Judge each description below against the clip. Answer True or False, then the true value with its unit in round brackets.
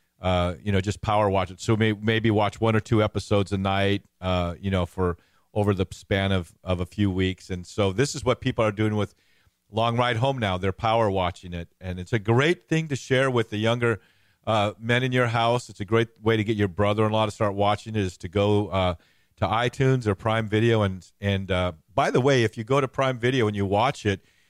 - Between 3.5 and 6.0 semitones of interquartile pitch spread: False (3.0 semitones)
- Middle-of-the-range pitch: False (105 Hz)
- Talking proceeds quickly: True (245 wpm)